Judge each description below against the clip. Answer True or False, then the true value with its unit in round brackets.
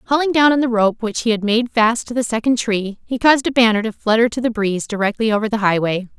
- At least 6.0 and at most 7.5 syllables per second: True (6.2 syllables/s)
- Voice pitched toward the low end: False (225 Hz)